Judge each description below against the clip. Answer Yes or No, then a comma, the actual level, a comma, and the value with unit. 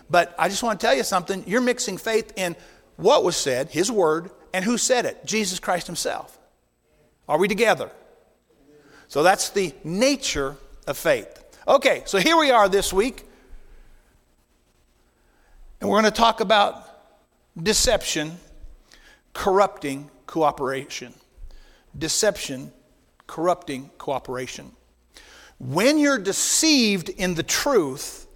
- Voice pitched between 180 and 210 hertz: Yes, medium, 185 Hz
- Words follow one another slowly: Yes, slow, 125 wpm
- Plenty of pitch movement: Yes, wide, 6.9 semitones